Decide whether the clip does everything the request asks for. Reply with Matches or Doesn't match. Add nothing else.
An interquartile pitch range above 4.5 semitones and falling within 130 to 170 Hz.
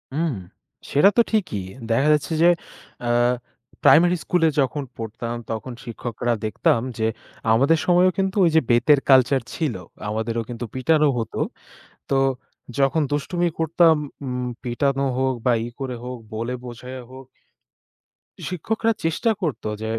Matches